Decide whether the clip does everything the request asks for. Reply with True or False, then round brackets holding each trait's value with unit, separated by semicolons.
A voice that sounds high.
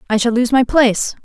True (240 Hz)